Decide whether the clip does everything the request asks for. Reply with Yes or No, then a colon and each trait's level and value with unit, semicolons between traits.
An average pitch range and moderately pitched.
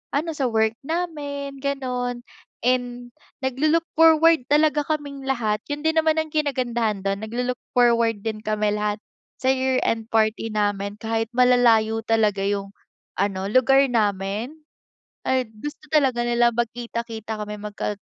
No: average, 4.2 semitones; high, 240 Hz